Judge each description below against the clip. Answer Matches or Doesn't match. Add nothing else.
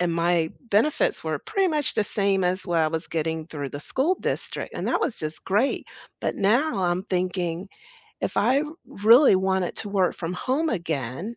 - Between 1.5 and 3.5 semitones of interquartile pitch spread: Doesn't match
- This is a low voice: Doesn't match